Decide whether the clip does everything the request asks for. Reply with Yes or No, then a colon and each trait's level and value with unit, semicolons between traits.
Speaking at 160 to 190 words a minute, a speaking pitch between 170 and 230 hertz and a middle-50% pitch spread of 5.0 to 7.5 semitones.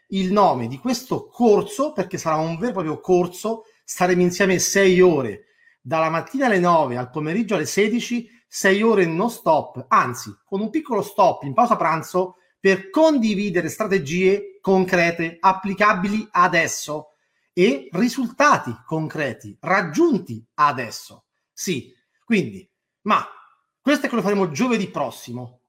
No: average, 135 wpm; high, 190 Hz; average, 5.3 semitones